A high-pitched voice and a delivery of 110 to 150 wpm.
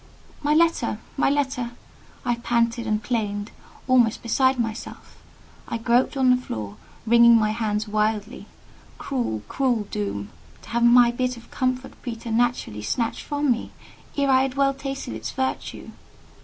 Yes: high, 235 Hz; average, 145 wpm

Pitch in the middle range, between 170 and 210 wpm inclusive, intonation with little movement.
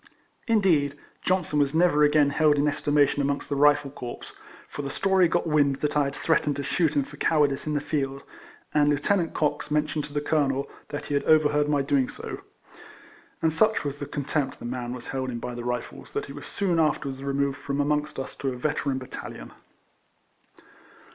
Yes: medium, 145 Hz; average, 200 wpm; narrow, 1.6 semitones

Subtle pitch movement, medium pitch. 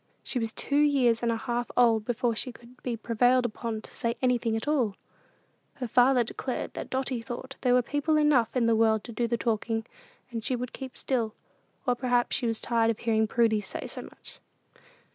No: narrow, 1.9 semitones; high, 240 Hz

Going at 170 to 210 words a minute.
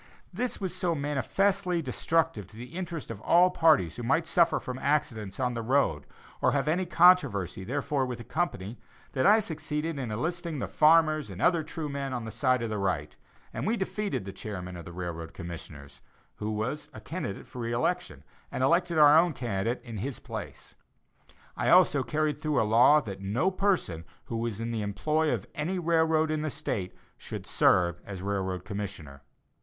Yes: average, 185 wpm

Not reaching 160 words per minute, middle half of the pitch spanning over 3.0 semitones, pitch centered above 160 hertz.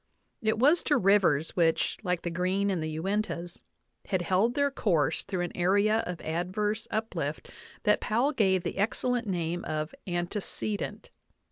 Yes: average, 150 wpm; average, 3.8 semitones; high, 190 Hz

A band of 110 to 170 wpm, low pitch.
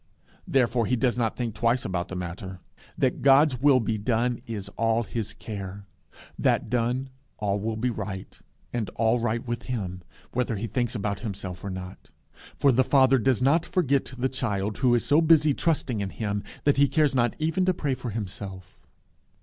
No: average, 185 wpm; low, 120 Hz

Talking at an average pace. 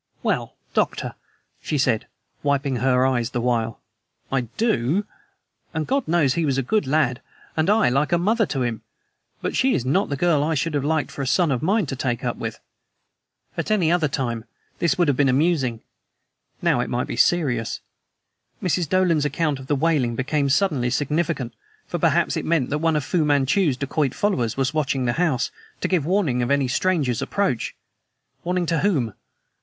Yes: average, 185 wpm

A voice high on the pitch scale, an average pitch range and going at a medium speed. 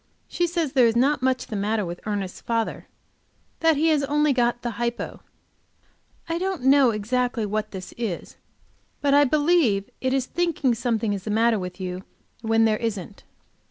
Yes: high, 240 Hz; average, 5.0 semitones; average, 175 wpm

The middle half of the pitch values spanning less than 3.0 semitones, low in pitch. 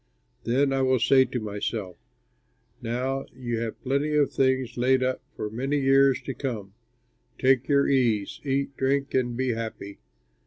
Yes: narrow, 2.6 semitones; low, 130 Hz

